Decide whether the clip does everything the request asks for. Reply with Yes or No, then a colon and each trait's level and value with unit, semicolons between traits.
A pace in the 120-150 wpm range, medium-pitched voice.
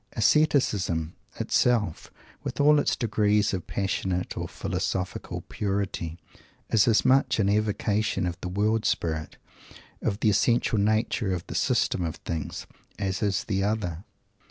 No: slow, 135 wpm; low, 100 Hz